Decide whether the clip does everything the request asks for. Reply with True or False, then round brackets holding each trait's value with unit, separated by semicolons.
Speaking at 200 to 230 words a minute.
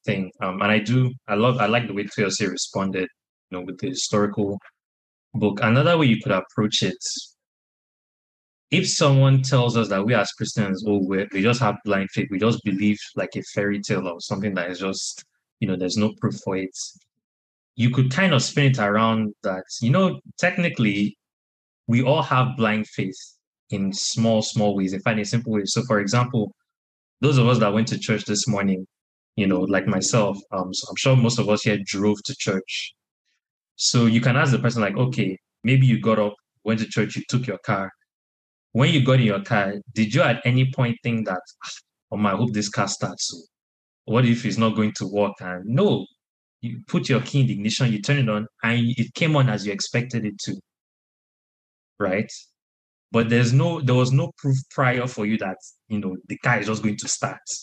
True (205 wpm)